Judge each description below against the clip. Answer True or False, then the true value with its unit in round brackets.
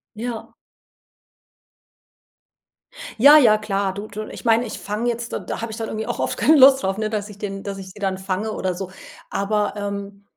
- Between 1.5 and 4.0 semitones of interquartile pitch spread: True (2.4 semitones)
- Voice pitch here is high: True (210 Hz)